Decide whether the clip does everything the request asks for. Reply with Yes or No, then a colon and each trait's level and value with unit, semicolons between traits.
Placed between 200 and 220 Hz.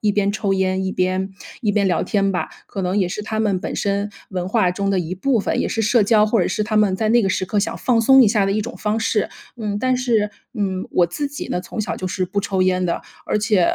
Yes: high, 205 Hz